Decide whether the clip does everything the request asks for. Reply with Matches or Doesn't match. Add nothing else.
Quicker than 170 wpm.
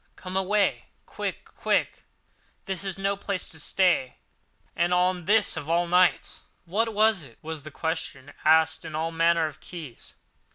Doesn't match